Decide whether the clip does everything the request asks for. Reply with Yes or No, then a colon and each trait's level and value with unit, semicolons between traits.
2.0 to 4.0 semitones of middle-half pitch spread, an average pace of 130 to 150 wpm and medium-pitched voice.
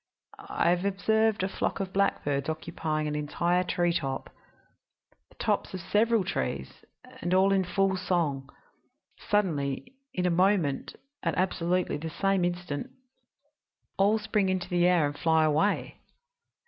Yes: average, 3.7 semitones; slow, 135 wpm; medium, 180 Hz